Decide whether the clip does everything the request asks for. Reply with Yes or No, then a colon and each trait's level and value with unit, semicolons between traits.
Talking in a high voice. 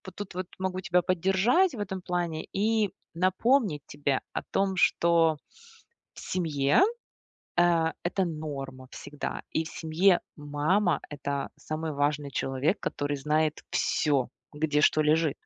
No: medium, 160 Hz